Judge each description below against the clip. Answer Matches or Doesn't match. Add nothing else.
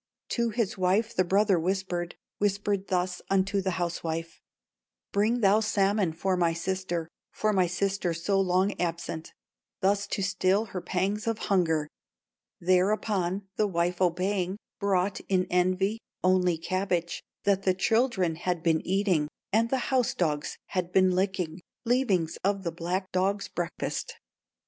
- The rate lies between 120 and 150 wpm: Matches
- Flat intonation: Matches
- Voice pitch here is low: Doesn't match